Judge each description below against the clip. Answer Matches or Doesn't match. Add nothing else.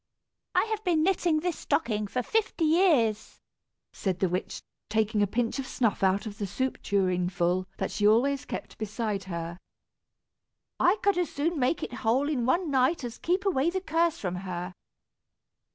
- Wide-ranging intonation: Matches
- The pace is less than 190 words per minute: Matches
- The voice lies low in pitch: Doesn't match